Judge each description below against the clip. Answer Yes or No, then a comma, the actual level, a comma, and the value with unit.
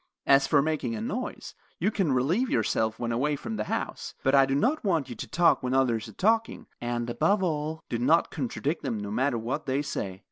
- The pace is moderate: No, fast, 220 wpm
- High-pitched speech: No, medium, 140 Hz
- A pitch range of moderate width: No, wide, 5.8 semitones